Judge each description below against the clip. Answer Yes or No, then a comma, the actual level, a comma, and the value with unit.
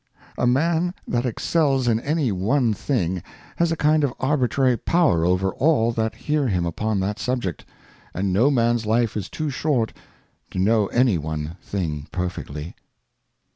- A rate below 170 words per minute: Yes, average, 155 wpm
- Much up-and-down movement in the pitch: Yes, wide, 6.7 semitones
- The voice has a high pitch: No, low, 115 Hz